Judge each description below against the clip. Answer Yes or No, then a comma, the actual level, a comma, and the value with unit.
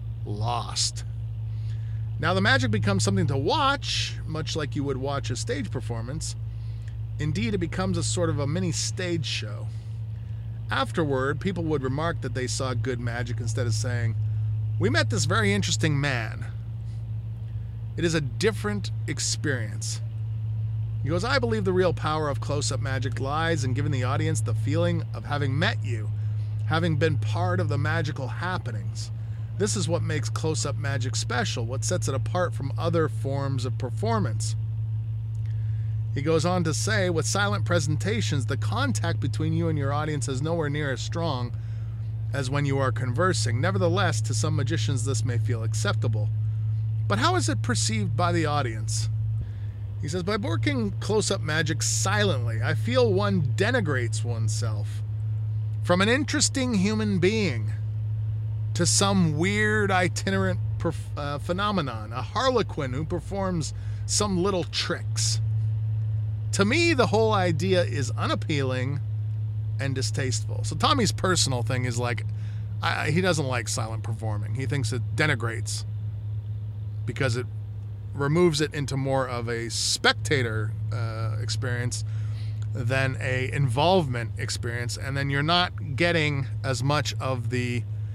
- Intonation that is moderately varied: No, narrow, 1.8 semitones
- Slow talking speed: No, average, 145 wpm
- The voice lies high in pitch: No, low, 110 Hz